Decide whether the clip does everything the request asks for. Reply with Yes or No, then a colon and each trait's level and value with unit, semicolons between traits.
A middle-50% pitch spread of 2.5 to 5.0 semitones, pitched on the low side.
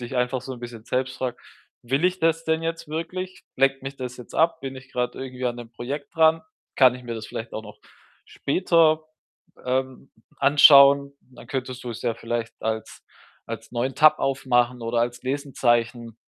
Yes: average, 2.8 semitones; low, 130 Hz